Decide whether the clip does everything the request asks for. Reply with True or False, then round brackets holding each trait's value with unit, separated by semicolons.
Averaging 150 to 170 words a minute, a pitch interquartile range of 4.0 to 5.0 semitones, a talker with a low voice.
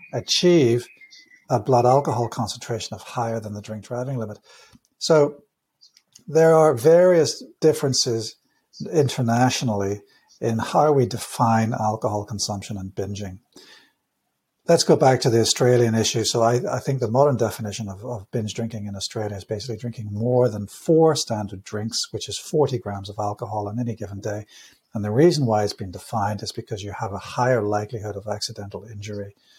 False (165 wpm; 3.5 semitones; 115 Hz)